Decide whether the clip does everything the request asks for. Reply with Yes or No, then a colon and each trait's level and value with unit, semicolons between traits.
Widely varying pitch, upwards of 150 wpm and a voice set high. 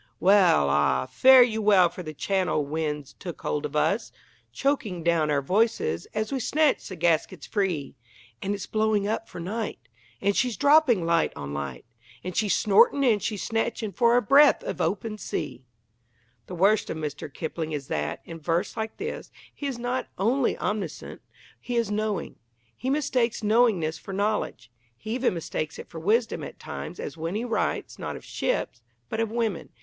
Yes: wide, 6.1 semitones; average, 180 wpm; high, 200 Hz